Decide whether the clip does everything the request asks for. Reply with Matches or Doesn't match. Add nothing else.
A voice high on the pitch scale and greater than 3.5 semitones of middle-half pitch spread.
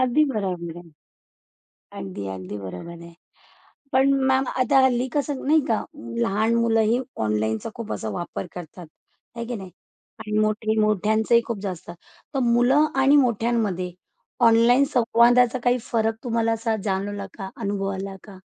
Matches